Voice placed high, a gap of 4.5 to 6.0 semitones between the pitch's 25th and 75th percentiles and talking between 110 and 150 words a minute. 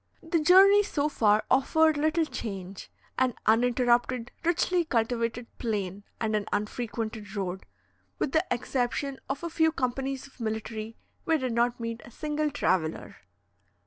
Yes: high, 245 Hz; average, 5.3 semitones; average, 140 wpm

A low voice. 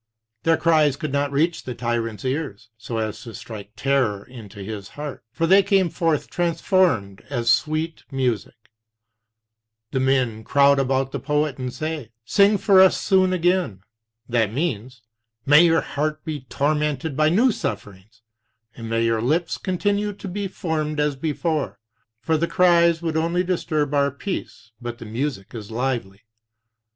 No: medium, 145 Hz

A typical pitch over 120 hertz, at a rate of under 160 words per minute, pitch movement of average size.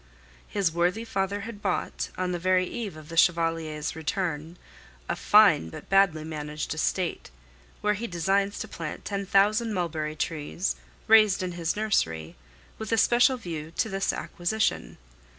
Yes: medium, 185 Hz; average, 150 wpm; average, 4.3 semitones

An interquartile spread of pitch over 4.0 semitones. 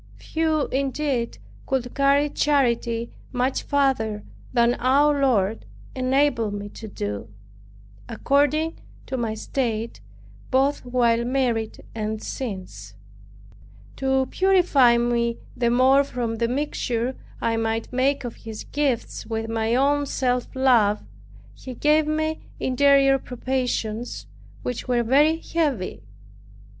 No: average, 3.4 semitones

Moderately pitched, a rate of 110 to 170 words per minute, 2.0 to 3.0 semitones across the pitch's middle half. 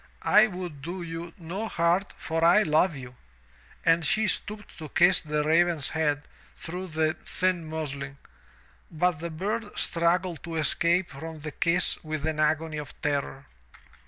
Yes: medium, 165 Hz; average, 155 wpm; narrow, 2.6 semitones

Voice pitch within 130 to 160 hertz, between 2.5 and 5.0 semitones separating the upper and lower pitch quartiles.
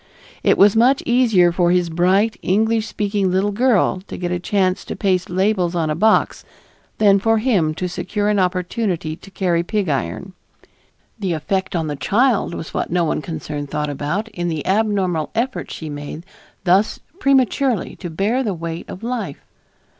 No: medium, 185 Hz; average, 4.0 semitones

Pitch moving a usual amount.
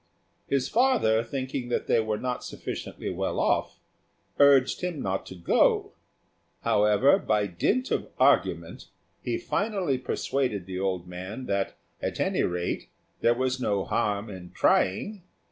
No: wide, 6.1 semitones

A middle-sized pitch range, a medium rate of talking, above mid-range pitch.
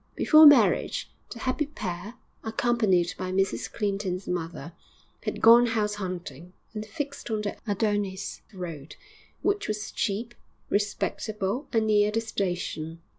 No: average, 3.7 semitones; slow, 125 wpm; high, 205 Hz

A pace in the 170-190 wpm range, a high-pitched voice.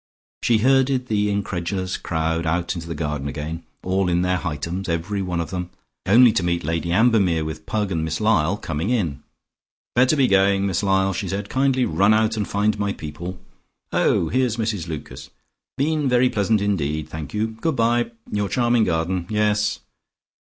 No: average, 175 wpm; very low, 95 Hz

